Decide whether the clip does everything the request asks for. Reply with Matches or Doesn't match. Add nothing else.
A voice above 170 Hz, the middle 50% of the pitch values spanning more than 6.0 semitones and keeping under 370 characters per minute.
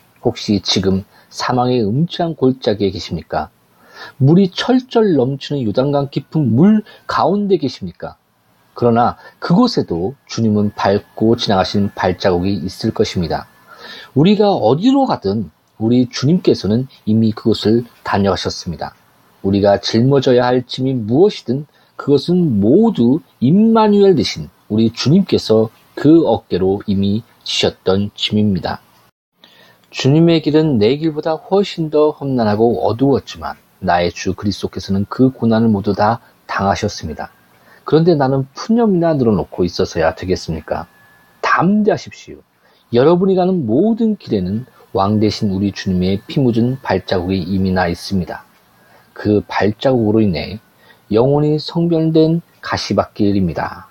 Doesn't match